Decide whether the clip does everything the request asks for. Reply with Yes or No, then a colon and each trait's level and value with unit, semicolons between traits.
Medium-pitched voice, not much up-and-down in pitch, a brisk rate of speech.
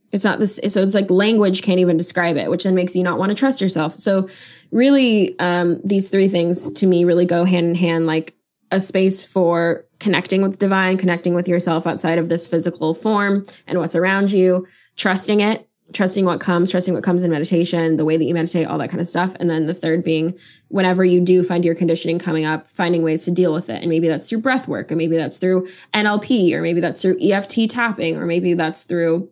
Yes: medium, 175 Hz; narrow, 2.3 semitones; fast, 230 wpm